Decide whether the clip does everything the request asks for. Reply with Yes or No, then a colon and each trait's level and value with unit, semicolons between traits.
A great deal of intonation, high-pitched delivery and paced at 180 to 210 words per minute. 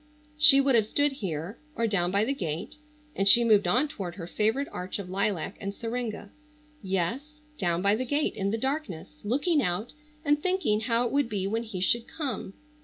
Yes: wide, 6.5 semitones; high, 225 Hz; average, 185 wpm